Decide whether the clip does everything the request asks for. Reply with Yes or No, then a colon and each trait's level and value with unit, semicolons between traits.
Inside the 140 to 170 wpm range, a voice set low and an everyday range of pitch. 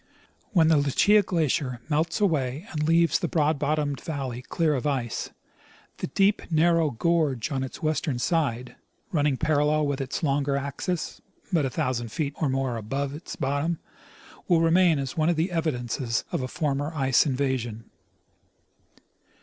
No: average, 155 wpm; medium, 145 Hz; average, 3.5 semitones